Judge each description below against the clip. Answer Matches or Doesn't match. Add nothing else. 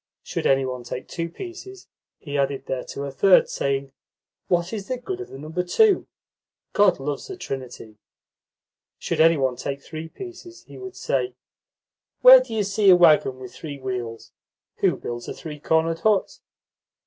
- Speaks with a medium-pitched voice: Matches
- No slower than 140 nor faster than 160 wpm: Doesn't match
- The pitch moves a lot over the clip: Matches